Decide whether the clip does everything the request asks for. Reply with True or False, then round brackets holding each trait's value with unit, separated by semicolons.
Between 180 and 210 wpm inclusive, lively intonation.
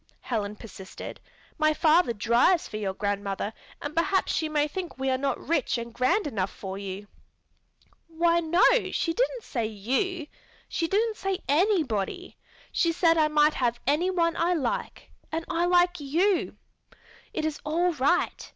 False (155 wpm; 6.9 semitones)